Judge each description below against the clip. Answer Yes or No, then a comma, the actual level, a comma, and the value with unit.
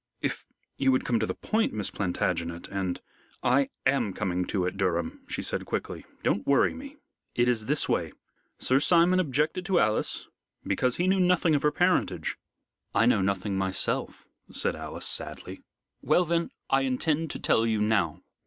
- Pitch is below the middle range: Yes, low, 125 Hz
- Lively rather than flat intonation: Yes, wide, 8.9 semitones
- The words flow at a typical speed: Yes, average, 175 wpm